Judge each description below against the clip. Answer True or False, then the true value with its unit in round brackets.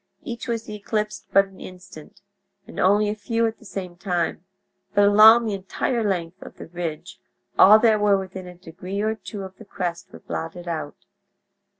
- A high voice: True (195 Hz)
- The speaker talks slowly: False (185 wpm)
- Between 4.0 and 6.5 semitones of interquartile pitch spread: False (3.1 semitones)